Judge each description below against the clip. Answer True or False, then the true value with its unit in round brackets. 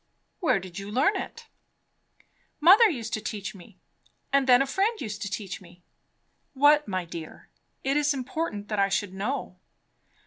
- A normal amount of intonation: False (6.5 semitones)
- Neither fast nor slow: True (165 wpm)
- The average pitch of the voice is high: True (220 Hz)